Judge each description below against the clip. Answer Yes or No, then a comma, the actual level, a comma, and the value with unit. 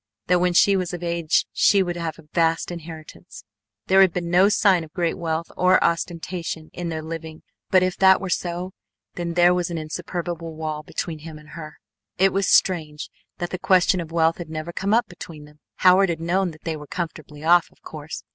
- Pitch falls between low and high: Yes, medium, 170 Hz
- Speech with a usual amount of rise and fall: No, narrow, 2.1 semitones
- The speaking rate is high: Yes, fast, 210 wpm